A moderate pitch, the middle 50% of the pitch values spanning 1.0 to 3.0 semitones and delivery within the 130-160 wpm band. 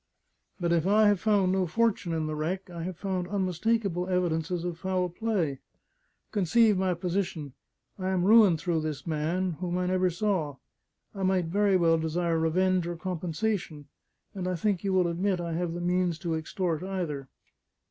No: medium, 180 Hz; narrow, 2.5 semitones; average, 175 wpm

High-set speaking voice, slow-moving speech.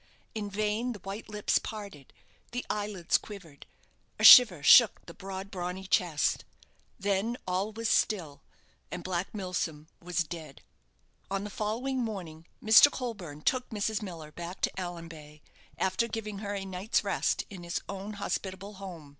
No: high, 195 Hz; average, 150 wpm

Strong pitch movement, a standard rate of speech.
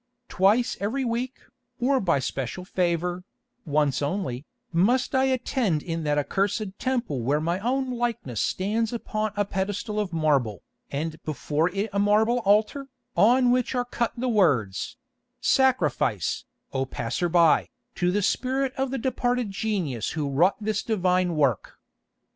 Yes: wide, 7.4 semitones; average, 145 wpm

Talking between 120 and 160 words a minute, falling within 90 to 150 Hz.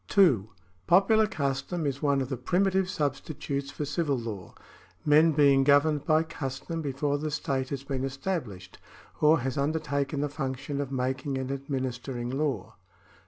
Yes: average, 150 wpm; medium, 140 Hz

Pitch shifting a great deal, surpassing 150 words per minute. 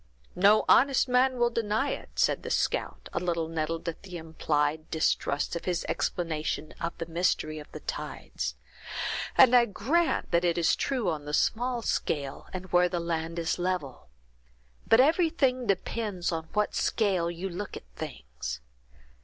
Yes: wide, 5.8 semitones; average, 160 wpm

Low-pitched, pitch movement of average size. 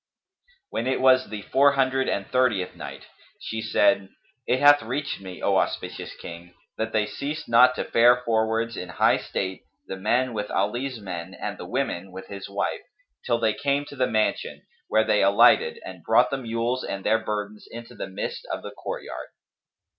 Yes: low, 115 Hz; average, 4.3 semitones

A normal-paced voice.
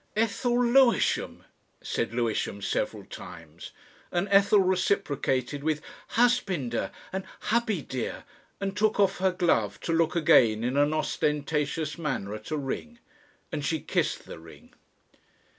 No: slow, 130 wpm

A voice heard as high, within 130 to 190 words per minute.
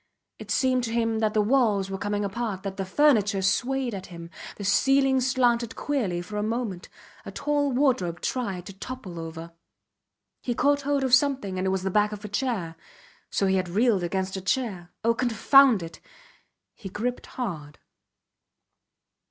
Yes: high, 210 Hz; average, 175 wpm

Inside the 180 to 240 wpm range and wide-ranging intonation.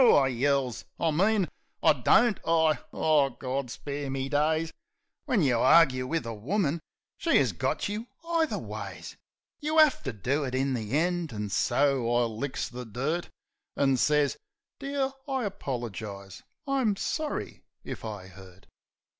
No: average, 155 wpm; wide, 6.1 semitones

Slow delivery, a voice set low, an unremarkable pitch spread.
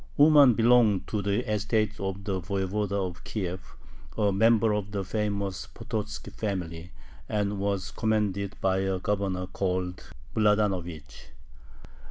No: slow, 125 wpm; low, 100 Hz; narrow, 2.2 semitones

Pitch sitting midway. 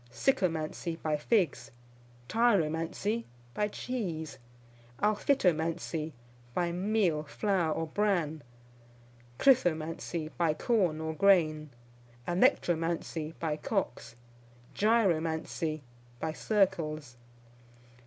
Yes: medium, 165 Hz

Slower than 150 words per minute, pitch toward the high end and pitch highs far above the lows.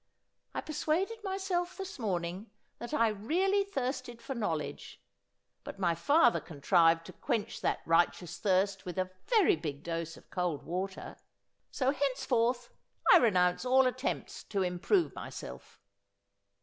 Yes: average, 140 wpm; high, 230 Hz; wide, 8.5 semitones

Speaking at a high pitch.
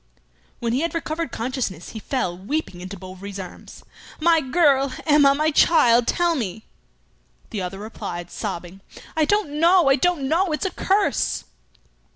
Yes: very high, 270 Hz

